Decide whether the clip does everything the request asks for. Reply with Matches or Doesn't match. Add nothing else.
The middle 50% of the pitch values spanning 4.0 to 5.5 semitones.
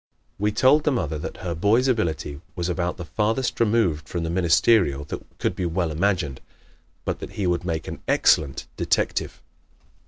Matches